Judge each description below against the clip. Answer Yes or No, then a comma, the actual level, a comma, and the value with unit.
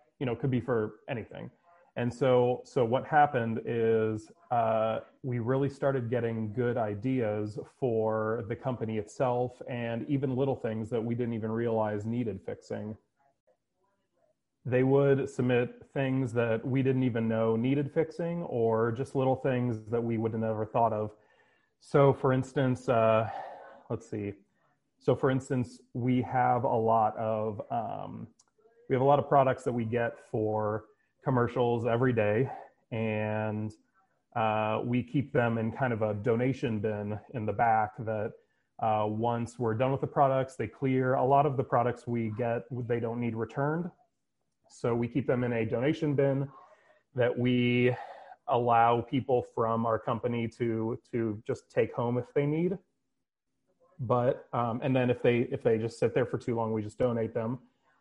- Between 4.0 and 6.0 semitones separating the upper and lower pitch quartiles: No, average, 2.8 semitones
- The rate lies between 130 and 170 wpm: Yes, average, 165 wpm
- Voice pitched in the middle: No, low, 120 Hz